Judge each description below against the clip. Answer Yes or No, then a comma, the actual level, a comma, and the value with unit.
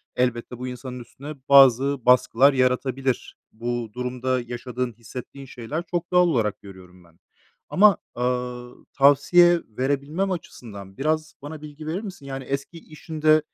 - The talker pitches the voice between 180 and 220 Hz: No, low, 130 Hz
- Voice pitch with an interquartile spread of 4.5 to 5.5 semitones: No, average, 3.9 semitones